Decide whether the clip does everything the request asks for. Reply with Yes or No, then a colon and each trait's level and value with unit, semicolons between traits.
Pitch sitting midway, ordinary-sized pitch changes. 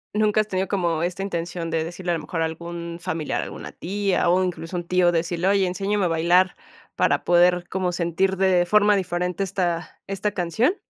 No: medium, 180 Hz; narrow, 2.1 semitones